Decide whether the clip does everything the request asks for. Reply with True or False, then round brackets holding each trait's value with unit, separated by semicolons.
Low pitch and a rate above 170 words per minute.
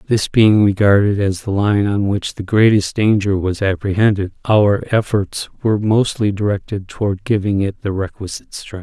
False (100 Hz; 165 wpm)